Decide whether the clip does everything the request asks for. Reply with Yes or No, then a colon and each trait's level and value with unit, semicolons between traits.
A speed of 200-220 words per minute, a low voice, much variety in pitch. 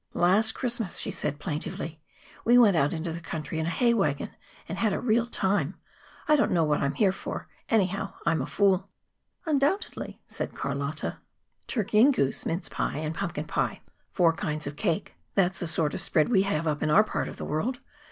No: fast, 205 wpm; medium, 180 Hz; wide, 5.8 semitones